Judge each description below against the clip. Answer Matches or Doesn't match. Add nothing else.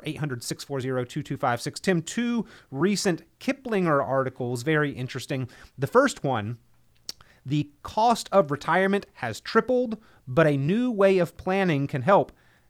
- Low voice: Doesn't match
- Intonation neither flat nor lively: Doesn't match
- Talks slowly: Matches